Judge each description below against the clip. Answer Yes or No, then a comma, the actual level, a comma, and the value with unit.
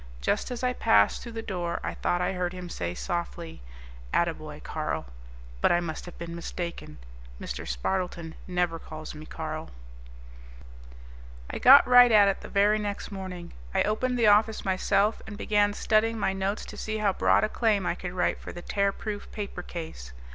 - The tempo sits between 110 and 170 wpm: No, average, 180 wpm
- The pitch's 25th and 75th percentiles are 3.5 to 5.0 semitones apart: Yes, average, 3.8 semitones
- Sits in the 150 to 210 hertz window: Yes, high, 190 Hz